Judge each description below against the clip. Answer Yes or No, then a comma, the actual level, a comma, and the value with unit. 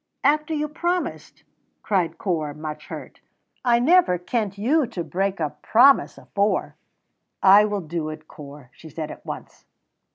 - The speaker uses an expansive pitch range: Yes, wide, 7.9 semitones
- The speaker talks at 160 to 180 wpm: No, average, 150 wpm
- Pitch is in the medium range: No, high, 195 Hz